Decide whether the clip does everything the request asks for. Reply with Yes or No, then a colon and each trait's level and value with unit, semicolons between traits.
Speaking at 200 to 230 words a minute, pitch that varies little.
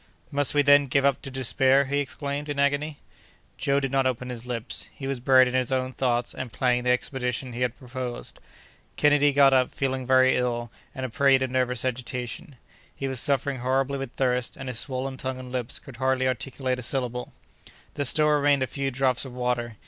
Yes: fast, 205 wpm; narrow, 1.7 semitones